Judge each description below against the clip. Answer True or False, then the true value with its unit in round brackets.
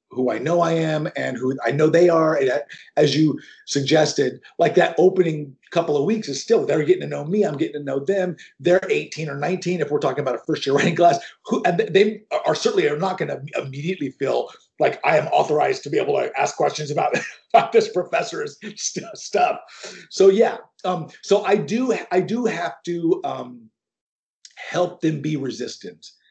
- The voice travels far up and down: True (5.8 semitones)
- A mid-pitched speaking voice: True (170 Hz)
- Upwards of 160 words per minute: True (200 wpm)